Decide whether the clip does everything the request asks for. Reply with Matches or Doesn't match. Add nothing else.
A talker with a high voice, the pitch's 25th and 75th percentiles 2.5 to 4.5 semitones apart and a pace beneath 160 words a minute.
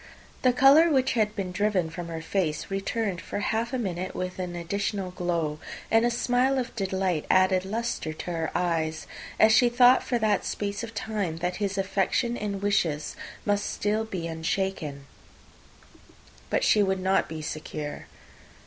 Doesn't match